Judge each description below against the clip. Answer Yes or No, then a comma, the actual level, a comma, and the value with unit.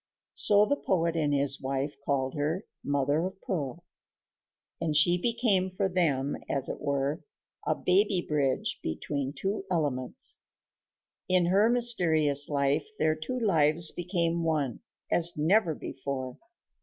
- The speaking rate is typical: No, slow, 130 wpm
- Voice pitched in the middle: Yes, medium, 160 Hz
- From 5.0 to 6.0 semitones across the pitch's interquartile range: No, average, 4.5 semitones